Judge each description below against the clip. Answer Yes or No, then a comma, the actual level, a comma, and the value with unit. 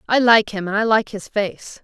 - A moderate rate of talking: No, fast, 260 wpm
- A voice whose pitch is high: Yes, high, 210 Hz